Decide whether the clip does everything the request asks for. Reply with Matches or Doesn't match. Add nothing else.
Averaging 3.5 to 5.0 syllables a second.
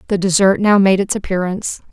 Doesn't match